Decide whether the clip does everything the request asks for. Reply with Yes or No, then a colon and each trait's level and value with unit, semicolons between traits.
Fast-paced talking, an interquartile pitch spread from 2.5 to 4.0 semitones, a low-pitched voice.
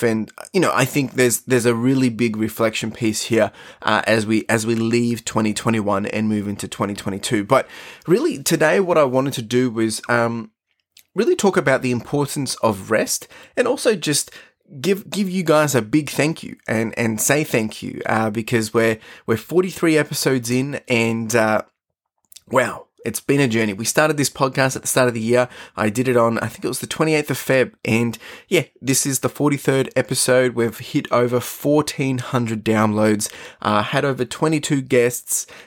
No: average, 185 wpm; average, 3.7 semitones; low, 125 Hz